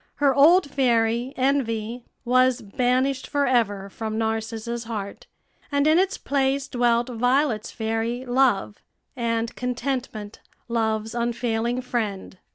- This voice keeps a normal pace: No, slow, 110 wpm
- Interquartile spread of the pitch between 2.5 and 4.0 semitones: Yes, average, 2.8 semitones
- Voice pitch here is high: Yes, high, 240 Hz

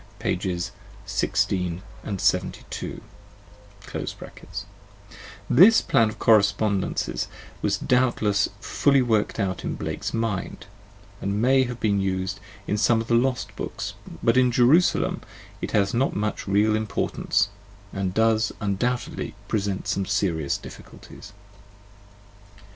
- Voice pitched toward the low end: Yes, low, 105 Hz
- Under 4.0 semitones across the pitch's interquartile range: Yes, average, 3.2 semitones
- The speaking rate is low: Yes, slow, 115 wpm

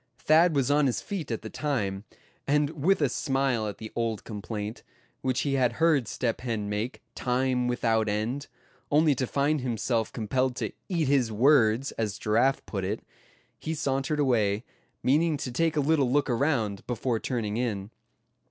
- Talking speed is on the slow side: No, average, 170 wpm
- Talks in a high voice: No, low, 125 Hz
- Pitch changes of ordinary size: Yes, average, 4.4 semitones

